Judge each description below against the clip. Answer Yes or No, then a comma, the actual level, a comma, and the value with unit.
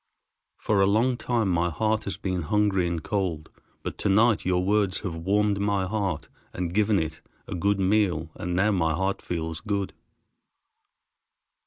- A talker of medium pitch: No, very low, 95 Hz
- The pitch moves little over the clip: No, average, 3.1 semitones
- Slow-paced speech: No, average, 165 wpm